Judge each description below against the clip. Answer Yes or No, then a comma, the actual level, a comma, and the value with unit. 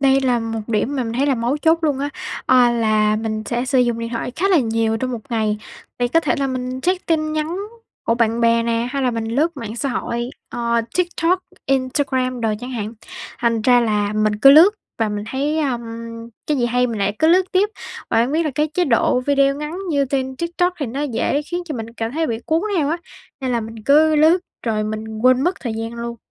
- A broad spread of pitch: No, average, 4.3 semitones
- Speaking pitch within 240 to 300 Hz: Yes, very high, 250 Hz